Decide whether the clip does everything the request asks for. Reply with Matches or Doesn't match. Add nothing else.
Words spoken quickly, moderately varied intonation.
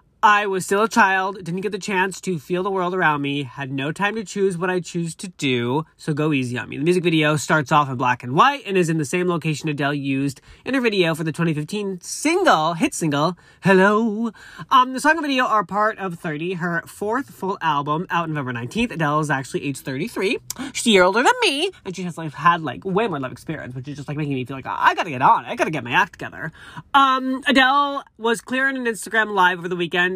Doesn't match